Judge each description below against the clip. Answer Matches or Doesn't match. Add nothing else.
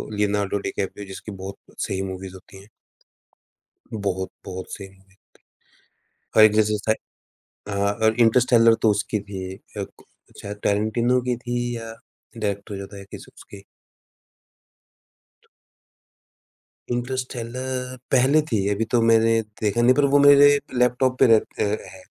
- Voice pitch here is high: Doesn't match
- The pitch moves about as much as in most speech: Matches